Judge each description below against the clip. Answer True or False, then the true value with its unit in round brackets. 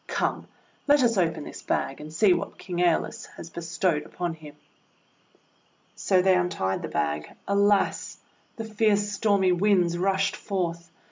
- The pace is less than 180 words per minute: True (150 wpm)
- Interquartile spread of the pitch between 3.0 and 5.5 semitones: True (3.5 semitones)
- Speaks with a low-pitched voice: False (180 Hz)